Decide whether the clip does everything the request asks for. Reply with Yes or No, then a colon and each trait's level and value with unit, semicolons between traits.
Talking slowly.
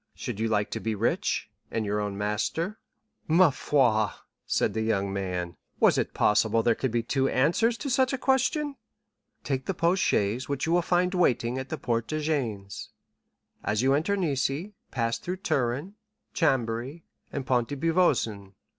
No: average, 170 wpm